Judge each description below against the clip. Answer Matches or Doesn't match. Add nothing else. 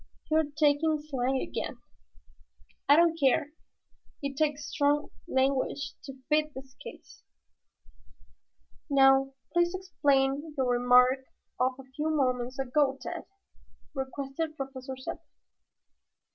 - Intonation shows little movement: Matches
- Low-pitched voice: Doesn't match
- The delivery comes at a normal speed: Doesn't match